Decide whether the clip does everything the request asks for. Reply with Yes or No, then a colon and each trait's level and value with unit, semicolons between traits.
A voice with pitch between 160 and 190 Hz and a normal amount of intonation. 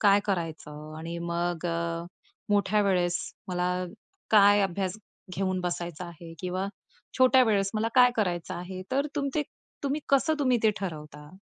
Yes: medium, 185 Hz; average, 3.7 semitones